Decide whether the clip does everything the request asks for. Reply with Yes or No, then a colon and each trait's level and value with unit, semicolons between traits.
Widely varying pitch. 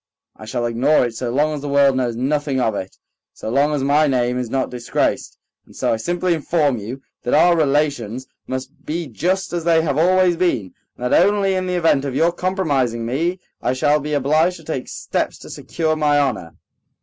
No: average, 4.7 semitones